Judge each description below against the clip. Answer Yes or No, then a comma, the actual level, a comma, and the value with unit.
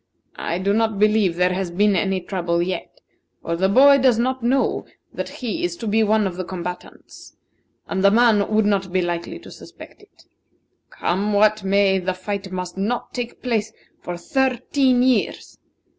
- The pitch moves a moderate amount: Yes, average, 3.9 semitones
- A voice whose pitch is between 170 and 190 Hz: No, high, 200 Hz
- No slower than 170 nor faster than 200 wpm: Yes, average, 175 wpm